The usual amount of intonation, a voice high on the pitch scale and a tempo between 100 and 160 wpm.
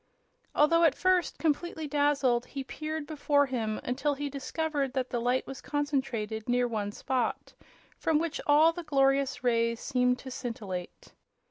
Yes: average, 3.4 semitones; very high, 275 Hz; average, 150 wpm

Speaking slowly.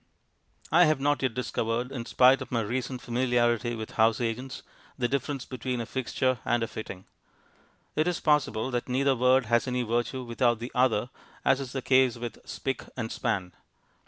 No: average, 180 wpm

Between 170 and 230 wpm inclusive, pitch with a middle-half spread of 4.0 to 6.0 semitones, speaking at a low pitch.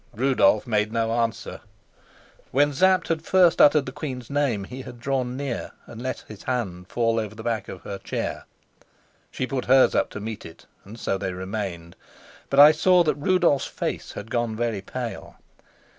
Yes: average, 180 wpm; average, 4.4 semitones; low, 120 Hz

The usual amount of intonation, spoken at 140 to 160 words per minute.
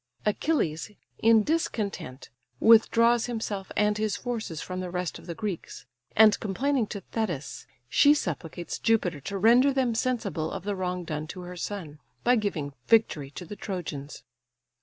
Yes: average, 4.8 semitones; average, 155 wpm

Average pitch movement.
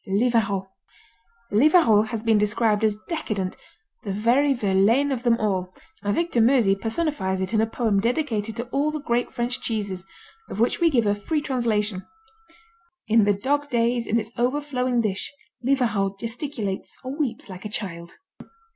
Yes: average, 3.7 semitones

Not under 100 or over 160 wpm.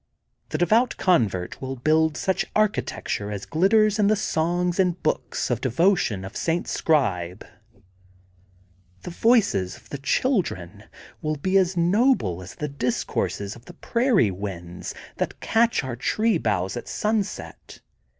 Yes: average, 140 wpm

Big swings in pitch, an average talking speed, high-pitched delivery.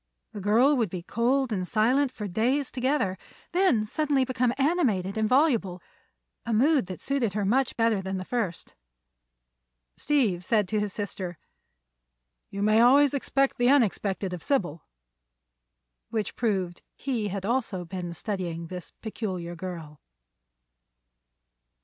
No: wide, 5.7 semitones; slow, 130 wpm; high, 215 Hz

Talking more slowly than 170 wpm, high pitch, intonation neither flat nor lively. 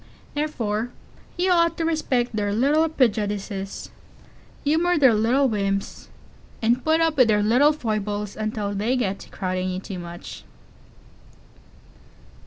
No: slow, 135 wpm; high, 225 Hz; wide, 6.2 semitones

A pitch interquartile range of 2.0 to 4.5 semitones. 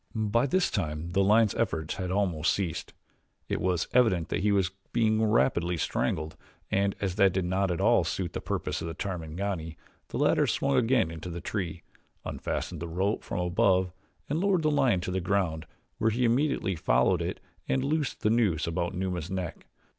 Yes: average, 4.2 semitones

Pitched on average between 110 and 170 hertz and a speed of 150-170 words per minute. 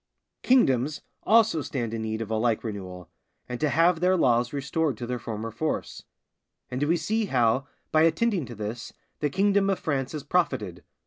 No: low, 135 Hz; average, 180 wpm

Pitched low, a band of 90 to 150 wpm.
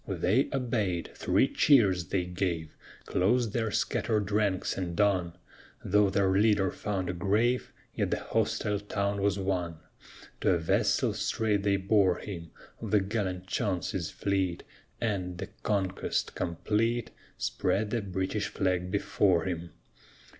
Yes: low, 100 Hz; slow, 135 wpm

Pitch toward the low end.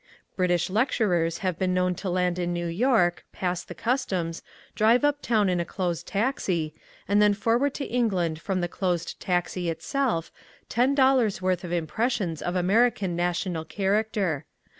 No: medium, 185 Hz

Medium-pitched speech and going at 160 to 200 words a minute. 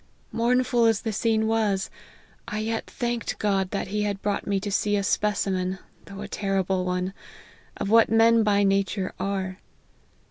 No: high, 205 Hz; average, 165 wpm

